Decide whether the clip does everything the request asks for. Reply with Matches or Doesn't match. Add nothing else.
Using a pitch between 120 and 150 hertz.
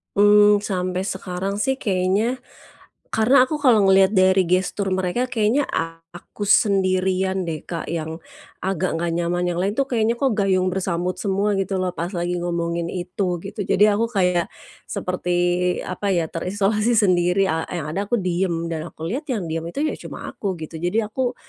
Doesn't match